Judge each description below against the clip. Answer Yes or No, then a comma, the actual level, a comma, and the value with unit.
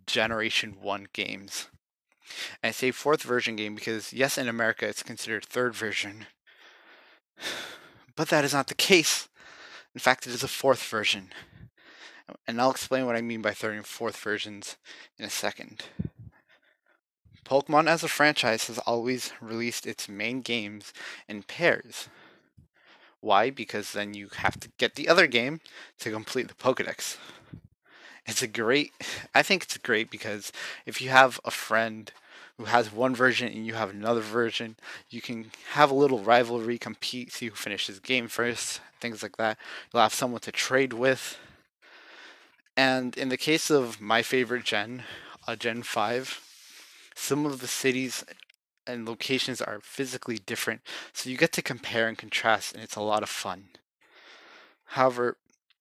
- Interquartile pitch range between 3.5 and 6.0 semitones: No, average, 3.0 semitones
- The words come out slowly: No, average, 160 wpm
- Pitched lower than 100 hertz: No, low, 120 Hz